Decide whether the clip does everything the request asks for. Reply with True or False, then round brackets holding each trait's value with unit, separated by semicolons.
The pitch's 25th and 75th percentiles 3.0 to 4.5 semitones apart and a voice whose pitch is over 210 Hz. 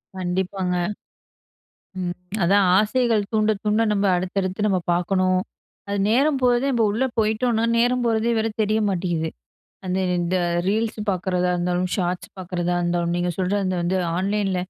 False (3.4 semitones; 195 Hz)